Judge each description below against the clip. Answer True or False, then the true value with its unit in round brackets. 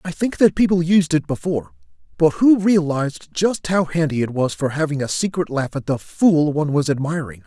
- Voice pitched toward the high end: False (155 Hz)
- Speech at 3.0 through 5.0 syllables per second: False (5.4 syllables/s)